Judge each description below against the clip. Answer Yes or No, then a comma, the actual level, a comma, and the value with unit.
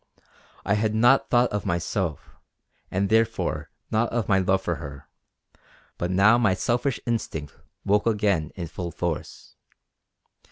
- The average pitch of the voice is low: Yes, low, 100 Hz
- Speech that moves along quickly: No, slow, 135 wpm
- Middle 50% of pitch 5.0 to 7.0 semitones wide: No, average, 4.5 semitones